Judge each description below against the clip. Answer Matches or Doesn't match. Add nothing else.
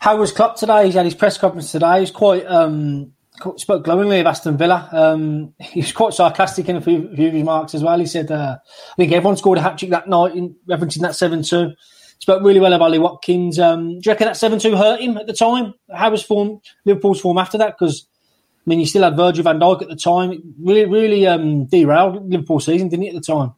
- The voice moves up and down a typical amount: Matches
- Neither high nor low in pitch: Matches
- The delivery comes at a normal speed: Doesn't match